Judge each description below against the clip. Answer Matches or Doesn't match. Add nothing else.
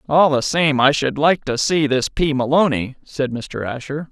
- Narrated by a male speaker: Matches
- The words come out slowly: Doesn't match